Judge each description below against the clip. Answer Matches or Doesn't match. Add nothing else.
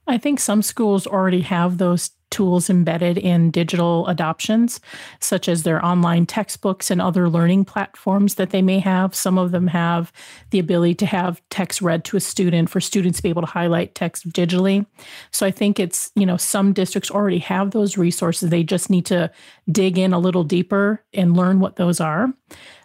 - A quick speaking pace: Doesn't match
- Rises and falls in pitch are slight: Matches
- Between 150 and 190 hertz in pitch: Matches